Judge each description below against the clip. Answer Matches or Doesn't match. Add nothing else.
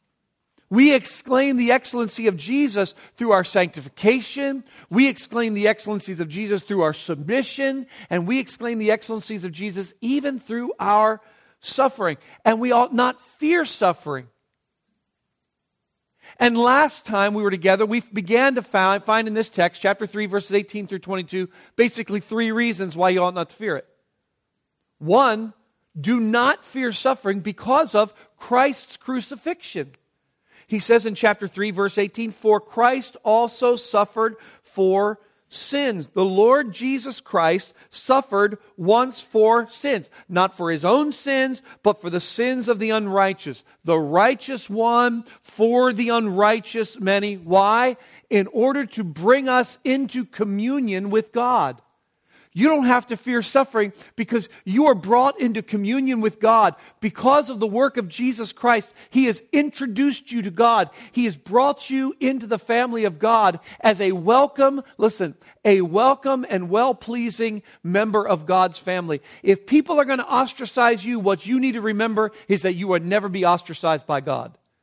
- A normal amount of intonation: Matches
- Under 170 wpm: Matches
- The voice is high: Matches